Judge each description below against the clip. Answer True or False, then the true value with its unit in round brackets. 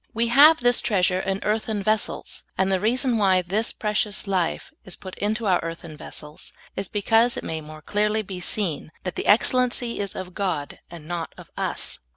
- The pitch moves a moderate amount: True (3.5 semitones)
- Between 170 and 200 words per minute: True (190 wpm)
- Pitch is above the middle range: True (200 Hz)